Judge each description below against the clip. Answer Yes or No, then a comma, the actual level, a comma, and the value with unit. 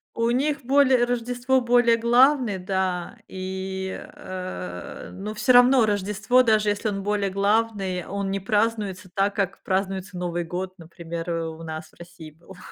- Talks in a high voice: Yes, high, 195 Hz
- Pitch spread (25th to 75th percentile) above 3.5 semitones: Yes, average, 4.1 semitones